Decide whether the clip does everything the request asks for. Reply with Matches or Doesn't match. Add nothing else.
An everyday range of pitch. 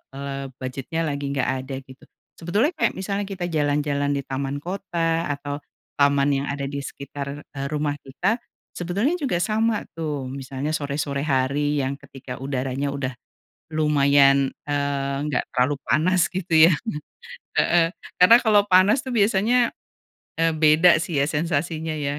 Matches